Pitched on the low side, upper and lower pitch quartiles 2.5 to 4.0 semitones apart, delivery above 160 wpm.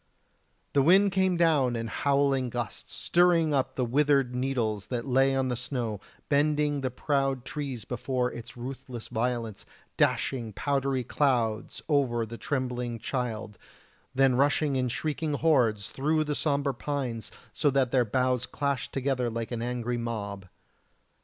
No: low, 130 Hz; average, 3.1 semitones; average, 145 wpm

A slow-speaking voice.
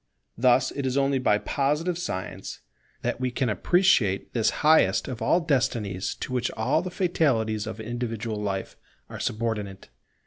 No: average, 150 wpm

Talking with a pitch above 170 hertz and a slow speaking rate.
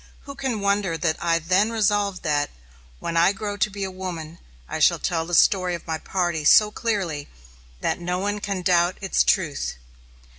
No: medium, 185 Hz; average, 185 wpm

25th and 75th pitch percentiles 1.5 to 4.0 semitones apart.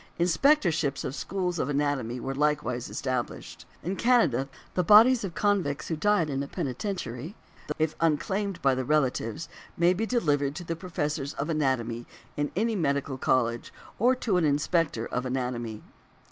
No: wide, 5.5 semitones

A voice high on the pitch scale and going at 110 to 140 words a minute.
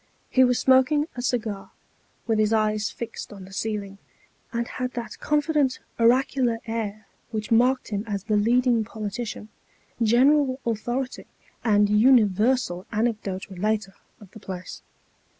Yes: high, 225 Hz; slow, 135 wpm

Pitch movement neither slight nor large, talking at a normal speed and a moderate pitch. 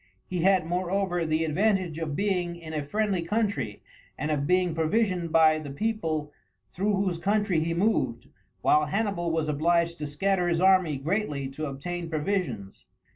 Yes: average, 3.7 semitones; average, 160 wpm; medium, 170 Hz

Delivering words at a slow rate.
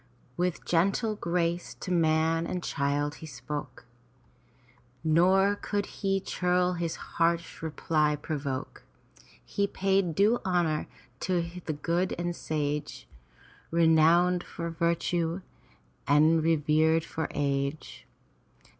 Yes: slow, 105 wpm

